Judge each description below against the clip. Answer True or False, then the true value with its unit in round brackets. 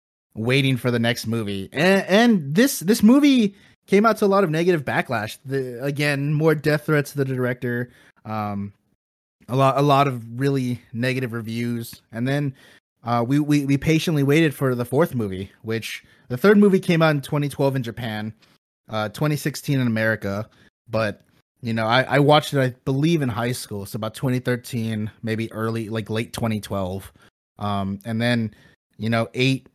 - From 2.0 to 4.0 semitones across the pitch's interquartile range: False (4.6 semitones)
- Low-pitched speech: True (125 Hz)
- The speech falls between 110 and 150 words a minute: False (185 wpm)